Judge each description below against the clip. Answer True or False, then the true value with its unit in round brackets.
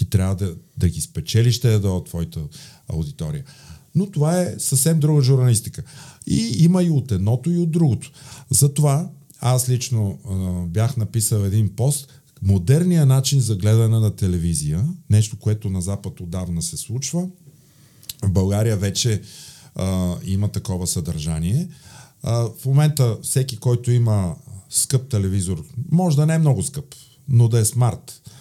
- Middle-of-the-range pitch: False (120 Hz)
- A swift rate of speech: False (150 wpm)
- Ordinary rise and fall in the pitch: False (6.2 semitones)